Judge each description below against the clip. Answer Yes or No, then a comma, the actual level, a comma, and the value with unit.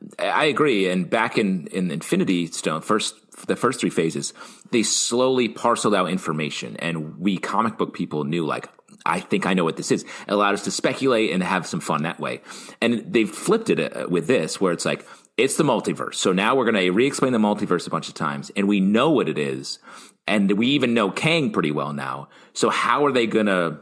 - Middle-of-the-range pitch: No, very low, 95 Hz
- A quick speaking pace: Yes, fast, 215 wpm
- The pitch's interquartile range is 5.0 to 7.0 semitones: Yes, wide, 5.5 semitones